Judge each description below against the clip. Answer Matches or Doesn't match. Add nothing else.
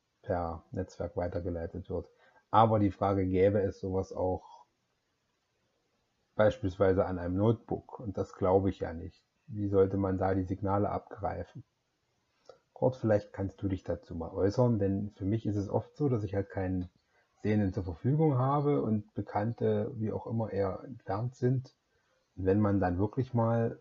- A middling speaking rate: Matches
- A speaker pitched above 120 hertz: Doesn't match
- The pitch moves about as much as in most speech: Matches